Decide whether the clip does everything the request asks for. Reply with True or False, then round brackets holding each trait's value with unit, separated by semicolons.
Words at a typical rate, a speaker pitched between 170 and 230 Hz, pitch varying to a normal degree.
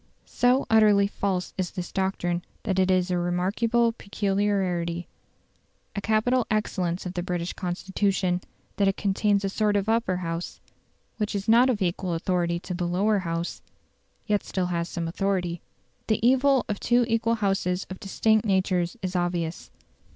True (160 wpm; 190 Hz; 3.1 semitones)